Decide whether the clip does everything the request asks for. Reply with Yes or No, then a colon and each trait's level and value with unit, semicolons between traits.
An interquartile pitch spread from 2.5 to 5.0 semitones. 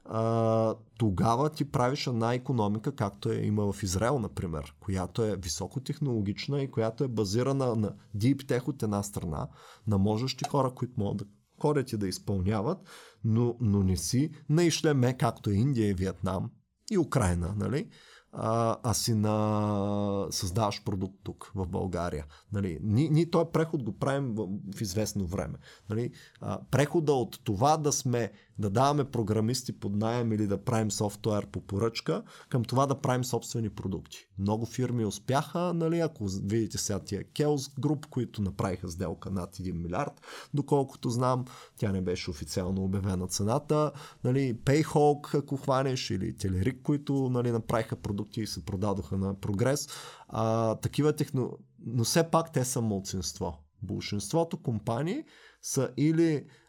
No: wide, 5.4 semitones